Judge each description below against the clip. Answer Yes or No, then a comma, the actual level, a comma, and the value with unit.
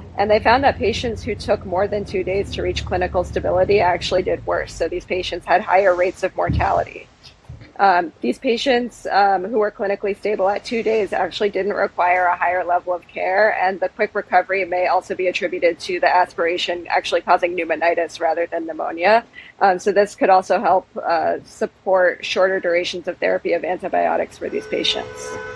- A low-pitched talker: No, medium, 185 Hz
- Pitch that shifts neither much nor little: No, narrow, 2.2 semitones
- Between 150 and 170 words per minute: No, average, 185 wpm